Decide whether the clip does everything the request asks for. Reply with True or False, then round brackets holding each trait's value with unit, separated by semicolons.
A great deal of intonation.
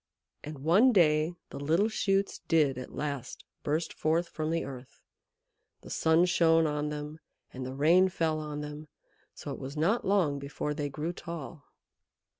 False (2.4 semitones)